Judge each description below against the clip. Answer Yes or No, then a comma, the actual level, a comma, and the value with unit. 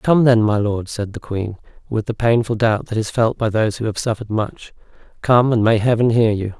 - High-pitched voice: No, low, 110 Hz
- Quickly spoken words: Yes, fast, 235 wpm